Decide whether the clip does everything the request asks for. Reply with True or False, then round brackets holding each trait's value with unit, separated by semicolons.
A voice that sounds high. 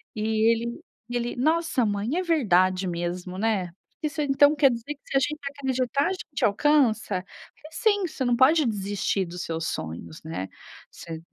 True (235 Hz)